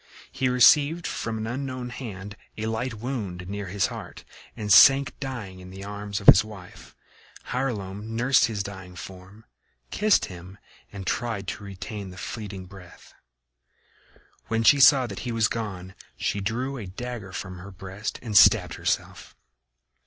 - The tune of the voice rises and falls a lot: No, average, 4.2 semitones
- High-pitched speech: No, low, 105 Hz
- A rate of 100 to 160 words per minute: Yes, average, 155 wpm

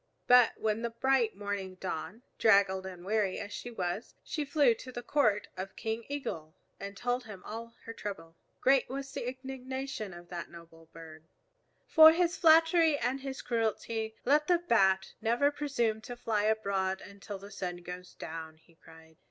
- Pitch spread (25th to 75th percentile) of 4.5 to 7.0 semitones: Yes, wide, 5.5 semitones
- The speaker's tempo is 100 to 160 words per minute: No, average, 170 wpm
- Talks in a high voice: Yes, high, 220 Hz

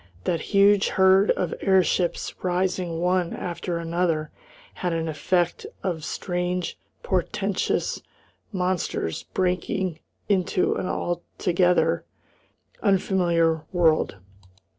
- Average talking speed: No, slow, 90 wpm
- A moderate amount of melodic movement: No, narrow, 1.8 semitones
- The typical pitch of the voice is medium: Yes, medium, 180 Hz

